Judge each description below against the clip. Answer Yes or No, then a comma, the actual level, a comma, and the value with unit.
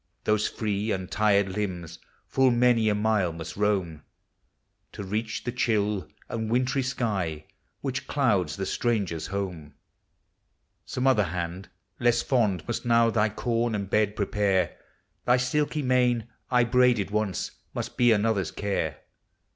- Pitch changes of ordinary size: Yes, average, 3.7 semitones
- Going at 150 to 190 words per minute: No, slow, 135 wpm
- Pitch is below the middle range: Yes, low, 105 Hz